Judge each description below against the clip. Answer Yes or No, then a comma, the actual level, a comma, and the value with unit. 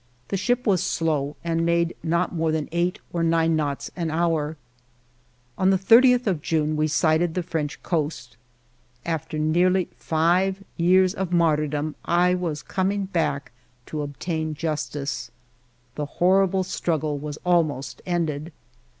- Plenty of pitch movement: No, average, 2.9 semitones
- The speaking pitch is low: No, medium, 165 Hz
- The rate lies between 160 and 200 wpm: No, average, 140 wpm